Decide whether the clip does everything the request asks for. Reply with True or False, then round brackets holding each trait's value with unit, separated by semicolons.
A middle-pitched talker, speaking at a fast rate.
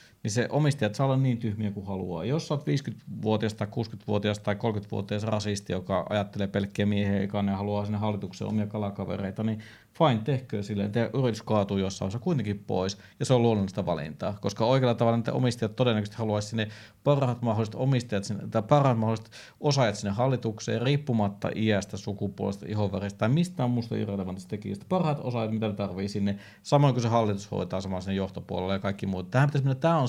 False (110 Hz; 180 wpm)